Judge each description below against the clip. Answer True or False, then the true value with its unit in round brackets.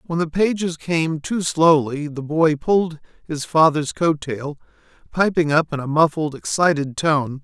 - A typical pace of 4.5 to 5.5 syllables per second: False (4.3 syllables/s)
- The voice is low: False (155 Hz)